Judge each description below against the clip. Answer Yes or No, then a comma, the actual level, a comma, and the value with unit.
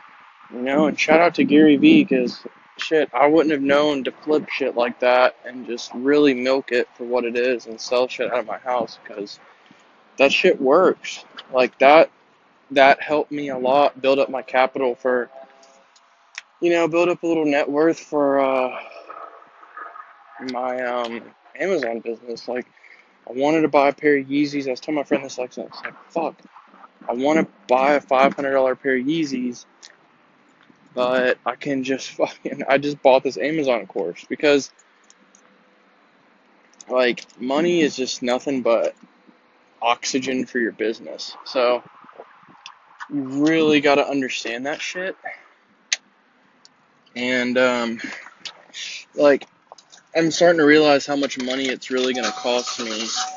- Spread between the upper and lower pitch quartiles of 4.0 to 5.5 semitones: No, average, 2.7 semitones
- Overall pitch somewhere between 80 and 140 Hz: Yes, low, 135 Hz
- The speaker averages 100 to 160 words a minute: Yes, average, 155 wpm